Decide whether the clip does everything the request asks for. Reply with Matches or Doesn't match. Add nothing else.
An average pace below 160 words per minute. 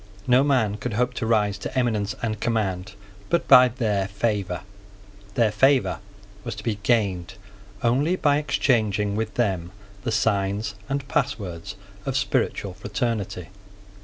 Matches